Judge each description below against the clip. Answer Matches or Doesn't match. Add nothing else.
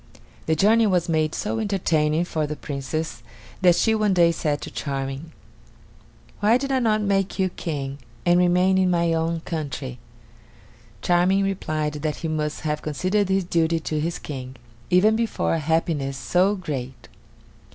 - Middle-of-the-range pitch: Matches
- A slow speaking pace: Doesn't match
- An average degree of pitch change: Matches